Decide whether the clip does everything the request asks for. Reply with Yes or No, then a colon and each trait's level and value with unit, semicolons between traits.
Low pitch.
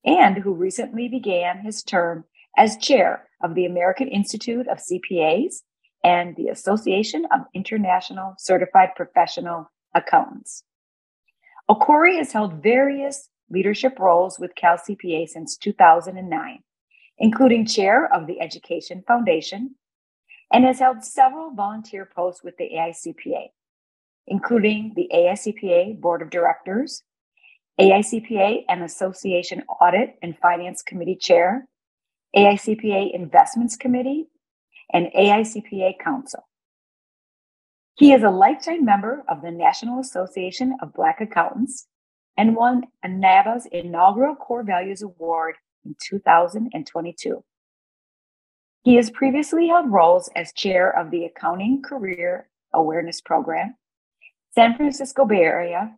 No: high, 200 Hz